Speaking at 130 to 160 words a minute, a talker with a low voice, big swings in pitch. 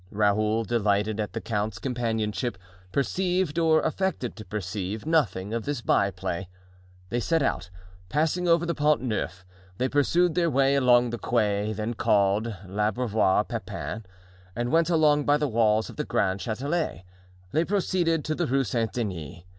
Yes: average, 155 wpm; low, 115 Hz; wide, 6.3 semitones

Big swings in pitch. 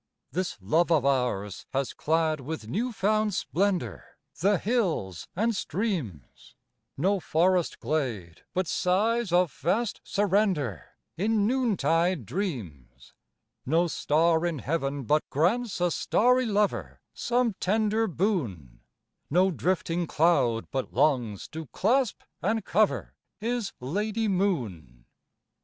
Yes: wide, 7.1 semitones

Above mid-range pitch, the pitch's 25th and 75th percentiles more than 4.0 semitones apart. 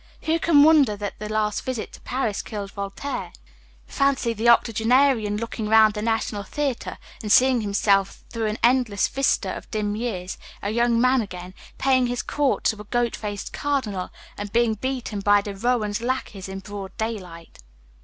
No: high, 220 Hz; average, 3.6 semitones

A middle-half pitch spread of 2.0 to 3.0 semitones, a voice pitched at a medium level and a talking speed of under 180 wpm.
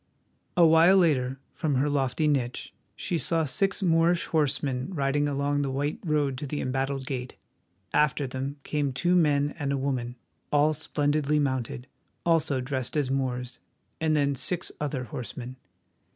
Yes: narrow, 2.6 semitones; medium, 145 Hz; average, 150 wpm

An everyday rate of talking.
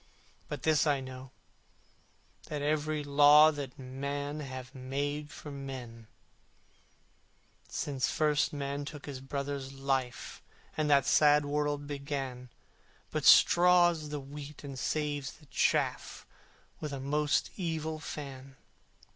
No: slow, 120 wpm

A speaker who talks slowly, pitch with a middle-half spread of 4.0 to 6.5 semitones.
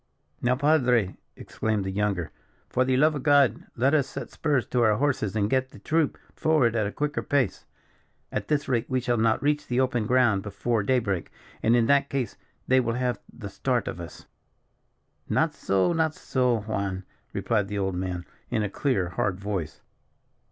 No: average, 185 wpm; average, 4.6 semitones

